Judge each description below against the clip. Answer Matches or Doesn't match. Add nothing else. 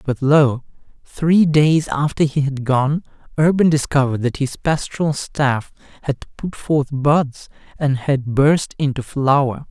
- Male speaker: Matches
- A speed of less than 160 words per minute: Matches